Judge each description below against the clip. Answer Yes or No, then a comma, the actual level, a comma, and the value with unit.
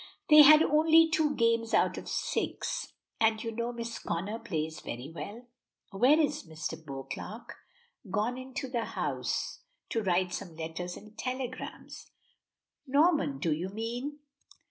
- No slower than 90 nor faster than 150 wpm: Yes, average, 145 wpm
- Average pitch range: No, wide, 6.7 semitones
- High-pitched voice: Yes, high, 230 Hz